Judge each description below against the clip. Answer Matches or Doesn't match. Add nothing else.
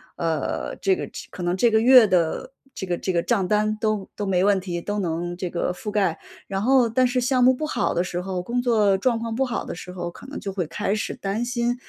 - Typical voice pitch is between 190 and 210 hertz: Matches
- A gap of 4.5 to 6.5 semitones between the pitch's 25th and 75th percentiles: Matches